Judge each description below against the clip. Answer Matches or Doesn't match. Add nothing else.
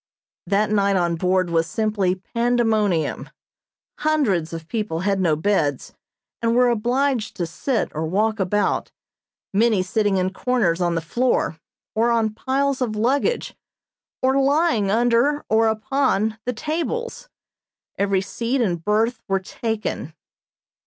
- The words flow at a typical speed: Doesn't match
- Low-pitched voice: Doesn't match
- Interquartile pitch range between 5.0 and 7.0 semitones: Doesn't match